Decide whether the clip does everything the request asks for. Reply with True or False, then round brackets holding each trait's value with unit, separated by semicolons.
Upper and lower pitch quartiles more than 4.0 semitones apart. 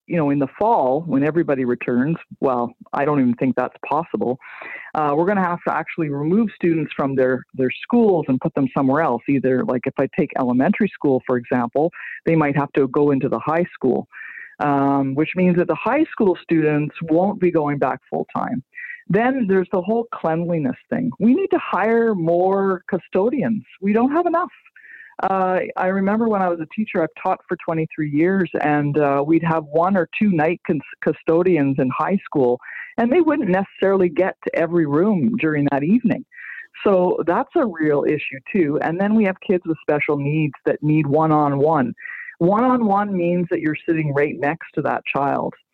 True (5.1 semitones)